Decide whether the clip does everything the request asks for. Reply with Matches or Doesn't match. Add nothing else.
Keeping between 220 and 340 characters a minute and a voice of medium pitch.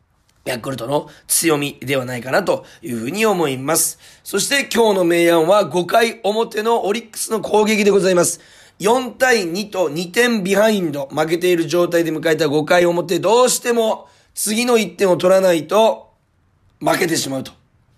Matches